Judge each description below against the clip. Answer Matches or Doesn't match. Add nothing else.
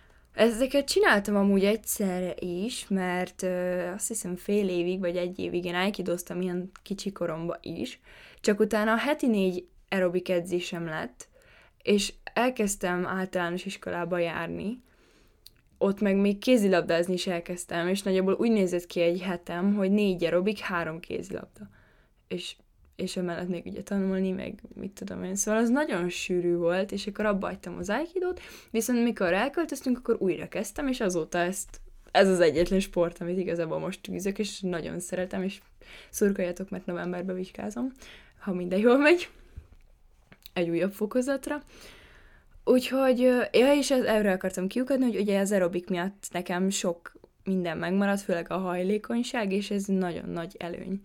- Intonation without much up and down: Doesn't match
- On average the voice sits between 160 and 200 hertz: Matches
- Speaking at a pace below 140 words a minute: Doesn't match